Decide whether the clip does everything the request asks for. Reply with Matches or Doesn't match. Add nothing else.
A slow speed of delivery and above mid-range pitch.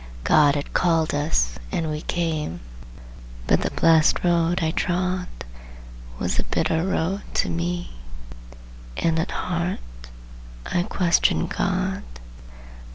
Doesn't match